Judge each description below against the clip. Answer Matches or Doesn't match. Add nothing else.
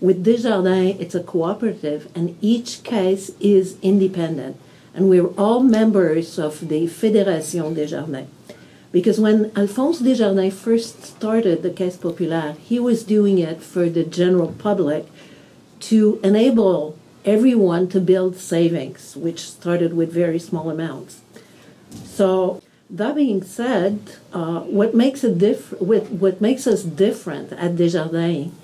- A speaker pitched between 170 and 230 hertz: Matches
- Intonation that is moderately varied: Matches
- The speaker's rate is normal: Doesn't match